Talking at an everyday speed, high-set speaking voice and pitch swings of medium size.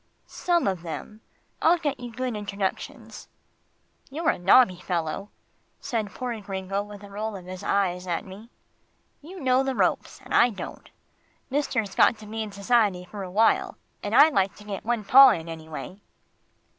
Yes: average, 170 wpm; high, 210 Hz; average, 4.5 semitones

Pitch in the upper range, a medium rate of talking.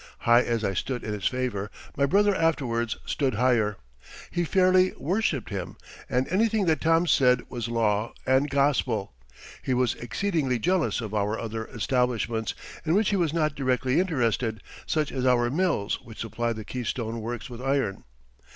No: low, 125 Hz; average, 165 wpm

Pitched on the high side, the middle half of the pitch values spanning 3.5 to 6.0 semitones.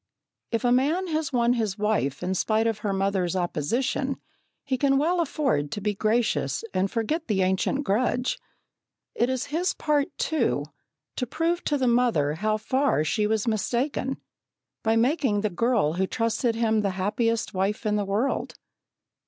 Yes: high, 230 Hz; average, 4.9 semitones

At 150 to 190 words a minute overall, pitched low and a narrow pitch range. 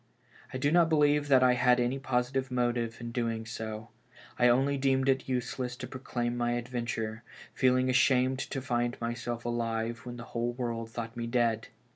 Yes: average, 175 wpm; low, 120 Hz; narrow, 1.7 semitones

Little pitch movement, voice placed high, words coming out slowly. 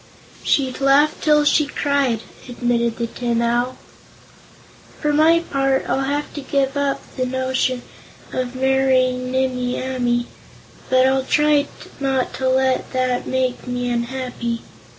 Yes: narrow, 1.8 semitones; very high, 260 Hz; slow, 130 wpm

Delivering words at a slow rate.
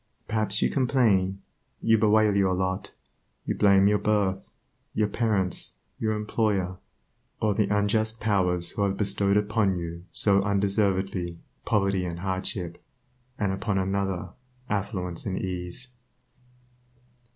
Yes: slow, 120 wpm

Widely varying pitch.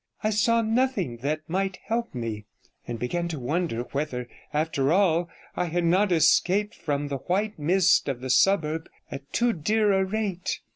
Yes: wide, 6.0 semitones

